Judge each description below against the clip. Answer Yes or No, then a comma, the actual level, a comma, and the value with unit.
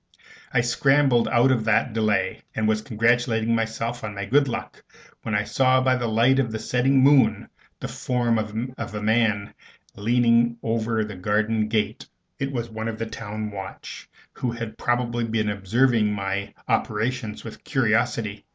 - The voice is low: Yes, low, 115 Hz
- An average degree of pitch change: No, narrow, 2.1 semitones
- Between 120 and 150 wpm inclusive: No, average, 165 wpm